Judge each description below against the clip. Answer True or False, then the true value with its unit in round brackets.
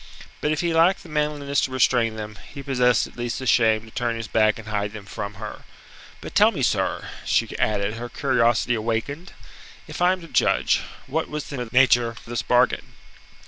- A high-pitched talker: False (120 Hz)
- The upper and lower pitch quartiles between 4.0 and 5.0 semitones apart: True (4.3 semitones)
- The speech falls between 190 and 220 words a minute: True (200 wpm)